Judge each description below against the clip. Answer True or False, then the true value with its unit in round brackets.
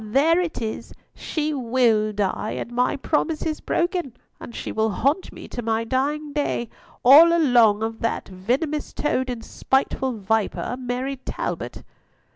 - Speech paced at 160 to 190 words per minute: False (150 wpm)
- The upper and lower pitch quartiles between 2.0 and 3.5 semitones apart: False (4.9 semitones)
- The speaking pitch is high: True (255 Hz)